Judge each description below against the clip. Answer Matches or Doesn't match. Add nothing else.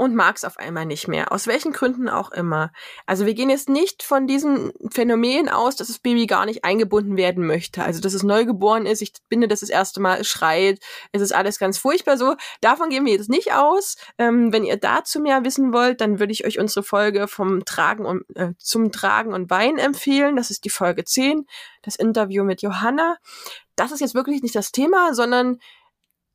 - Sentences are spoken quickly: Matches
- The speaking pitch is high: Matches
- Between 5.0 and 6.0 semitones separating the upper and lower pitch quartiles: Matches